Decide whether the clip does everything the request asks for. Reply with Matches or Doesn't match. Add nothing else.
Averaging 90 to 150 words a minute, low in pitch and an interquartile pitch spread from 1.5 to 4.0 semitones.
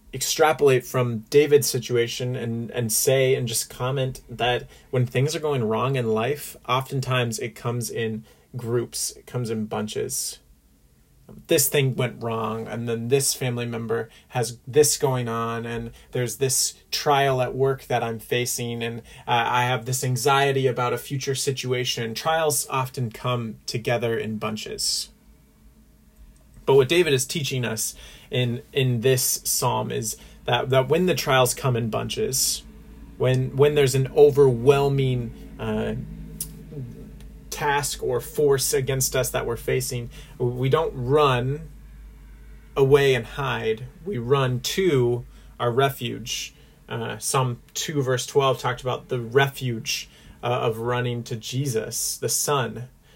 Matches